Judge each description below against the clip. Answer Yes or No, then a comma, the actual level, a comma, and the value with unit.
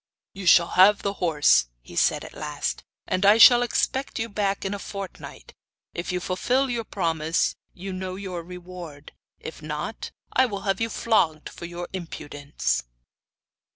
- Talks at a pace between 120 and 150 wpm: No, average, 160 wpm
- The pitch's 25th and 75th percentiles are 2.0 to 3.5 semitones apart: Yes, average, 3.1 semitones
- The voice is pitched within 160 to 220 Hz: Yes, medium, 185 Hz